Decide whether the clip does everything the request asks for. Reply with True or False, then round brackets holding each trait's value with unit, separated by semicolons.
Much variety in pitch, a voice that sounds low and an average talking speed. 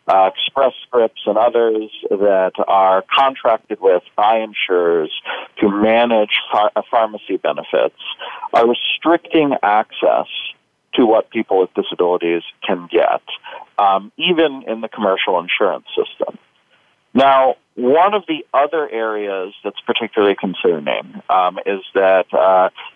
False (6.1 semitones; 110 Hz; 120 wpm)